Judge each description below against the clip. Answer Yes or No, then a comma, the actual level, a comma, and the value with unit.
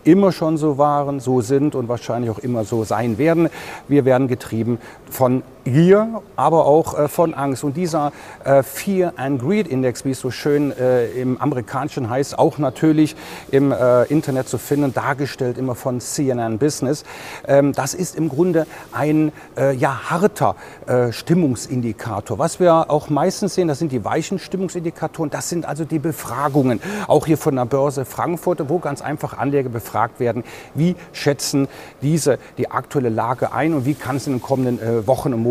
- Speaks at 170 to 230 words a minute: Yes, average, 175 wpm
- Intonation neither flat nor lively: Yes, average, 3.8 semitones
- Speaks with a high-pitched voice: No, medium, 140 Hz